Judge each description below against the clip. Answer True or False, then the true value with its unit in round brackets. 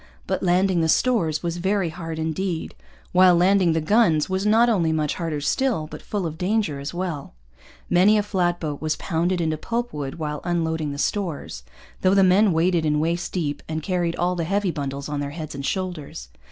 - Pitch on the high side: False (170 Hz)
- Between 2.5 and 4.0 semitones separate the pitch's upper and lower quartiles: True (3.3 semitones)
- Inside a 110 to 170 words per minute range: False (195 wpm)